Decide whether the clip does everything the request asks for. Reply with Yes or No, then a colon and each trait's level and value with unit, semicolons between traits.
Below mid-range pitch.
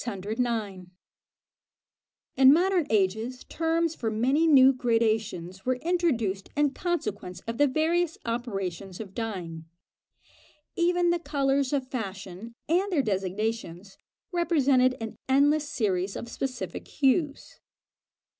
No: very high, 255 Hz